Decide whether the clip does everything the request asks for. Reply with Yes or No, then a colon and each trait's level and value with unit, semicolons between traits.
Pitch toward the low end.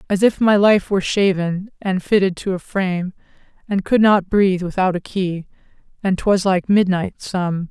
No: high, 190 Hz